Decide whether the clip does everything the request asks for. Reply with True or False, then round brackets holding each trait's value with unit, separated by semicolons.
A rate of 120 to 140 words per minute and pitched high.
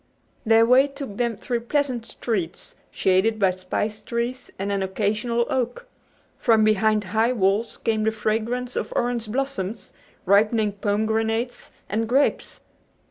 True (135 wpm; 225 Hz)